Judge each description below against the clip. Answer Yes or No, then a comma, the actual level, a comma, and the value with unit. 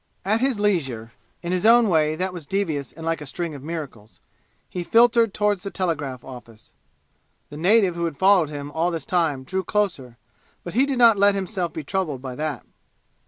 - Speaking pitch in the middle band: Yes, medium, 170 Hz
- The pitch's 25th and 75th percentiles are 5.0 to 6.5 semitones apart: Yes, wide, 5.4 semitones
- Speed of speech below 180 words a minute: No, average, 195 wpm